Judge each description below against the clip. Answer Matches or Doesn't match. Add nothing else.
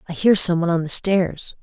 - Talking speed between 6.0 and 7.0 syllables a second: Doesn't match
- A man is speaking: Doesn't match